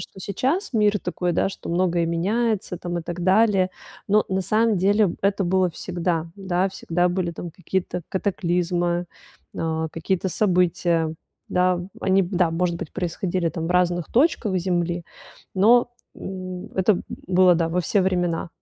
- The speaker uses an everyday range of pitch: No, narrow, 1.9 semitones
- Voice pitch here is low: No, medium, 180 Hz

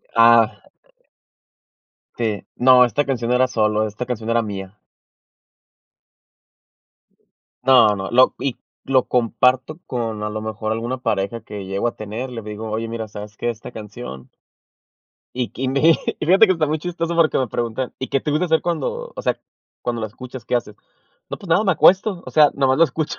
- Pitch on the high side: No, low, 120 Hz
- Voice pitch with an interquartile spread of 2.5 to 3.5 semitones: No, average, 4.2 semitones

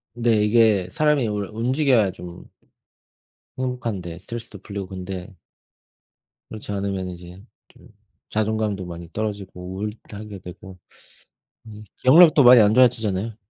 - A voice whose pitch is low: Yes, low, 105 Hz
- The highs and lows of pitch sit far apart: No, average, 3.6 semitones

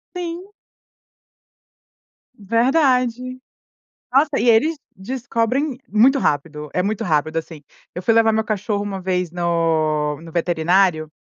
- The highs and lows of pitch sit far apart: Yes, wide, 7.0 semitones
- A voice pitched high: Yes, high, 205 Hz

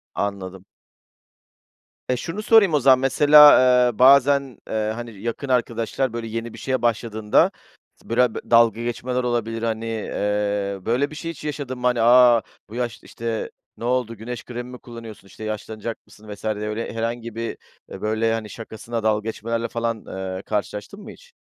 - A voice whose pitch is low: Yes, low, 115 Hz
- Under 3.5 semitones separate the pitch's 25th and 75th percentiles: Yes, narrow, 2.4 semitones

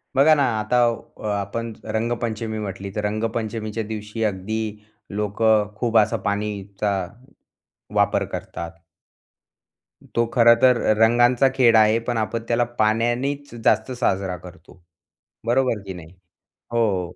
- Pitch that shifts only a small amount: Yes, narrow, 2.3 semitones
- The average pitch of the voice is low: Yes, low, 110 Hz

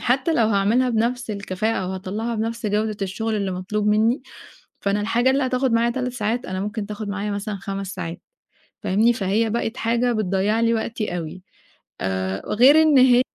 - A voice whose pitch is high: Yes, high, 215 Hz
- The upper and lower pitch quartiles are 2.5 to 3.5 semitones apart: Yes, average, 3.1 semitones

